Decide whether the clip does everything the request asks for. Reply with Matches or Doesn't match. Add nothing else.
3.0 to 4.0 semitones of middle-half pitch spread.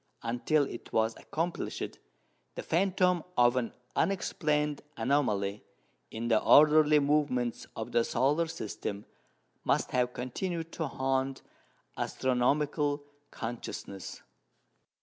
Doesn't match